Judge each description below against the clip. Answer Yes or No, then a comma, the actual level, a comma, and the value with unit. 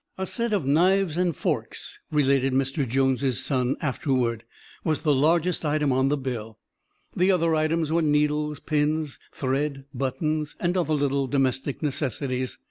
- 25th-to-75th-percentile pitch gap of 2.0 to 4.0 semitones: Yes, average, 3.0 semitones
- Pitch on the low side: No, medium, 145 Hz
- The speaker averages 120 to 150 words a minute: Yes, average, 145 wpm